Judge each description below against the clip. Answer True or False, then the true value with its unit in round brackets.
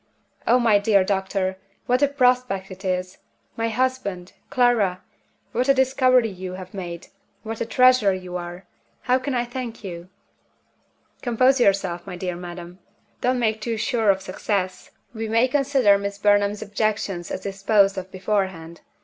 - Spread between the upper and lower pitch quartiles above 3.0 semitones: True (4.6 semitones)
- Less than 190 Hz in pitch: False (205 Hz)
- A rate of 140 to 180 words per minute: True (155 wpm)